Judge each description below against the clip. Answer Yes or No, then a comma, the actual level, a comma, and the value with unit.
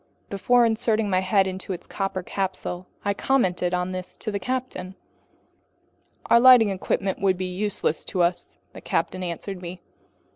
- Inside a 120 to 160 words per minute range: Yes, average, 155 wpm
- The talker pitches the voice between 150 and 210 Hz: Yes, high, 190 Hz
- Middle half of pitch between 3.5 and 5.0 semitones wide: No, narrow, 2.6 semitones